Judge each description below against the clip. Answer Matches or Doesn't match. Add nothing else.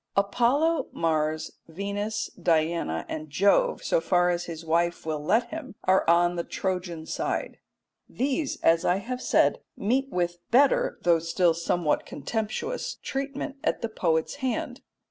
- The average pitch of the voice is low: Doesn't match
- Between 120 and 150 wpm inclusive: Matches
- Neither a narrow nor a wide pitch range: Doesn't match